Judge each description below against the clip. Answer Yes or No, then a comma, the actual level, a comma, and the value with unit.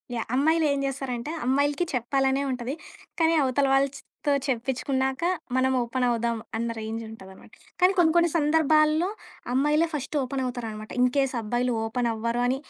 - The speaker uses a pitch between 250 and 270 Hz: Yes, very high, 265 Hz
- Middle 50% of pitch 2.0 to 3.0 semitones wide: No, average, 3.4 semitones